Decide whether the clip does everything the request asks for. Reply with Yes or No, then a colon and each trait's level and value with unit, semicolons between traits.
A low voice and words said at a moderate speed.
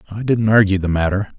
No: low, 100 Hz; fast, 215 wpm